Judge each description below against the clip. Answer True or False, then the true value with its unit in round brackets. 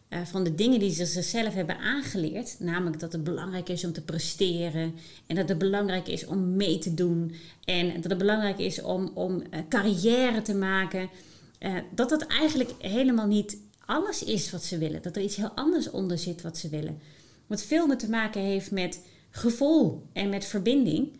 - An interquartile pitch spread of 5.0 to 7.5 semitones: False (4.3 semitones)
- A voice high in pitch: True (195 Hz)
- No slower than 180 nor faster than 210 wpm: True (195 wpm)